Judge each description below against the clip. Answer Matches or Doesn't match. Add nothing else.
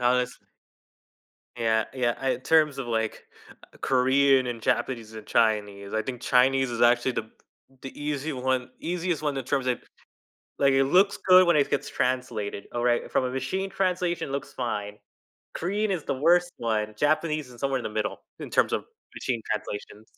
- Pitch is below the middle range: Matches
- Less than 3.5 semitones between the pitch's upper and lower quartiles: Doesn't match